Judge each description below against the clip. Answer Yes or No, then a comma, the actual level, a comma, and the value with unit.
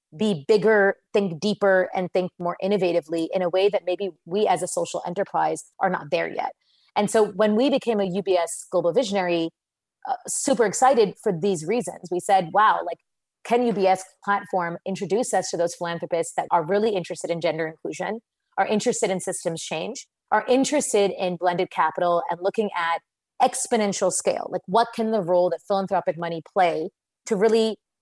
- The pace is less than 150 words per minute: No, average, 175 wpm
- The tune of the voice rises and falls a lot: No, average, 3.4 semitones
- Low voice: No, high, 190 Hz